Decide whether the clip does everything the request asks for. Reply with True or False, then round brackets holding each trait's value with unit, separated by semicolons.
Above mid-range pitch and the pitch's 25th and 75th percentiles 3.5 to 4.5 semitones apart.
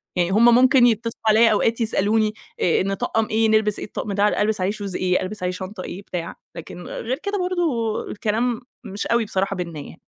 False (215 Hz; 3.0 semitones)